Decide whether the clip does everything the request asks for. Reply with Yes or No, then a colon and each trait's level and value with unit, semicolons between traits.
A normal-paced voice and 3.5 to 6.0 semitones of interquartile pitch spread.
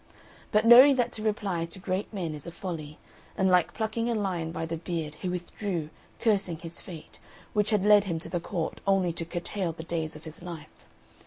No: fast, 210 wpm; average, 3.9 semitones